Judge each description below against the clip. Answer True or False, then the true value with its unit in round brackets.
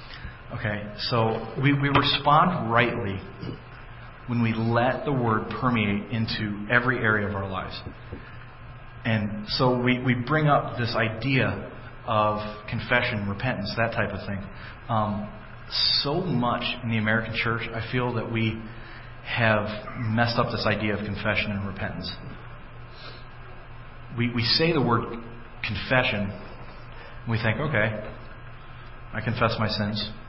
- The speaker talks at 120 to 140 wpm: True (135 wpm)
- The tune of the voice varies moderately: False (2.0 semitones)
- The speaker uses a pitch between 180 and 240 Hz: False (115 Hz)